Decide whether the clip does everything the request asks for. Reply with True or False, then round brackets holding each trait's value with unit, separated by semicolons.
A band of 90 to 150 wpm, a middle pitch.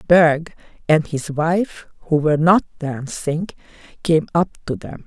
True (140 wpm; 160 Hz)